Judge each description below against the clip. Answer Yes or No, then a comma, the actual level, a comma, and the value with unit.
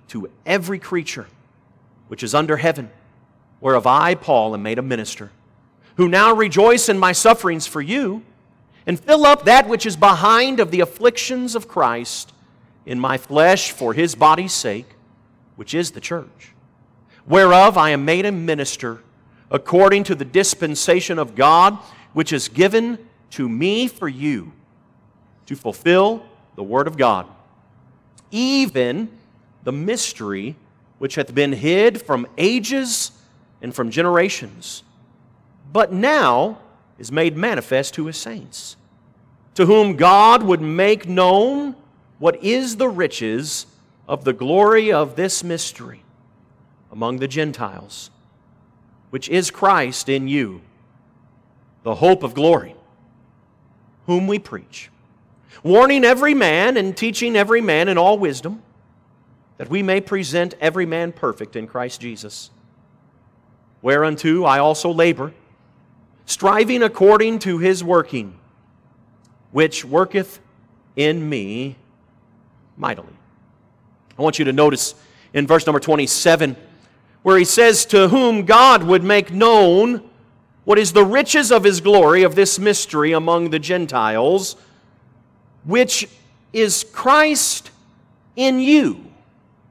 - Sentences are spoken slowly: Yes, slow, 130 wpm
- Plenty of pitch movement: Yes, wide, 8.2 semitones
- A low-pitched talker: No, medium, 160 Hz